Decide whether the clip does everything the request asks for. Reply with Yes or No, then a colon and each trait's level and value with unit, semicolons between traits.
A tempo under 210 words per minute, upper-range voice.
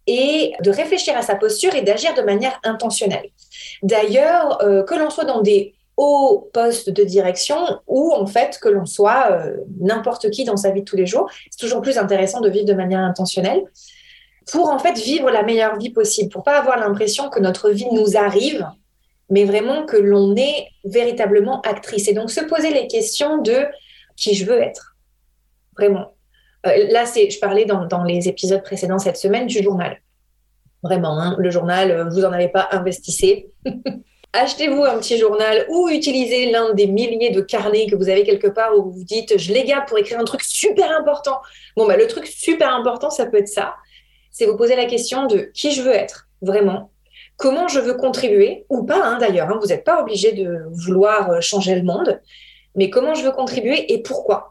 Yes: average, 200 wpm; high, 225 Hz